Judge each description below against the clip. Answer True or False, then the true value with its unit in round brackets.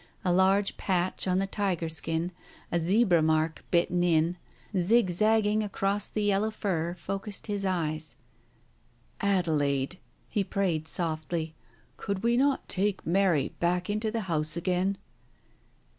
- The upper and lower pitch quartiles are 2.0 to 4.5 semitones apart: True (3.4 semitones)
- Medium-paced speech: False (130 wpm)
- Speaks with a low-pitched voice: False (185 Hz)